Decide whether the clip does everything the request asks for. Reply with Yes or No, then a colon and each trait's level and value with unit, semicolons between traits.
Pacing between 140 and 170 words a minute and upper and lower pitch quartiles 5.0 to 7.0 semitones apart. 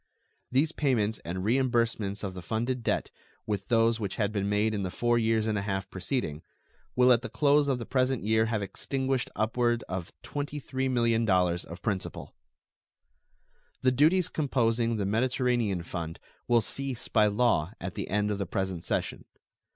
No: average, 165 wpm; average, 4.2 semitones